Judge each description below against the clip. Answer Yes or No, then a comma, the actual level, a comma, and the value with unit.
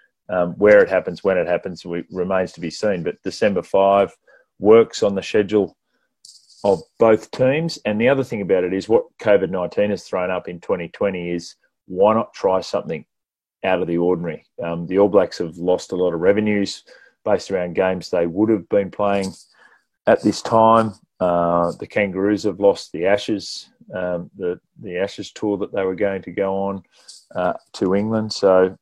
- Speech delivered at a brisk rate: No, average, 185 wpm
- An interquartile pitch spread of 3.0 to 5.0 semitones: No, narrow, 2.6 semitones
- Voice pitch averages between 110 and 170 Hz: No, very low, 95 Hz